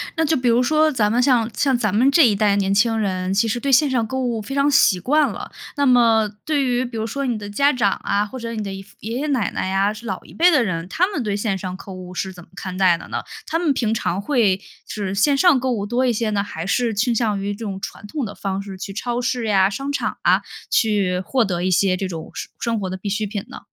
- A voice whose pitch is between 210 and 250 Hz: Yes, high, 220 Hz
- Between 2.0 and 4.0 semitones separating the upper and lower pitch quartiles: No, average, 4.4 semitones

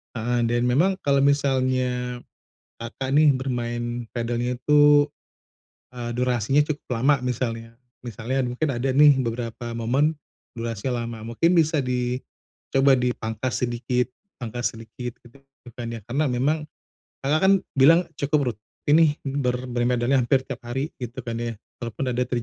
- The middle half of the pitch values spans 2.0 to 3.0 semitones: Yes, narrow, 2.5 semitones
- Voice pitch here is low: Yes, low, 125 Hz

